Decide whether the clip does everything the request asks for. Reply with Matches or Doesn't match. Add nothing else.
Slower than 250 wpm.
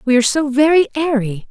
Matches